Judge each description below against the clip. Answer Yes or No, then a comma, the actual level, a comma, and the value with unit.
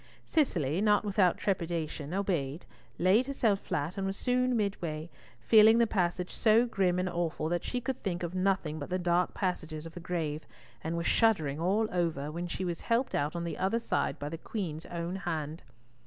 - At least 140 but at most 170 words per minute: No, average, 190 wpm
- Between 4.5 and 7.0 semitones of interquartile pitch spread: No, average, 3.8 semitones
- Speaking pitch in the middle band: Yes, medium, 175 Hz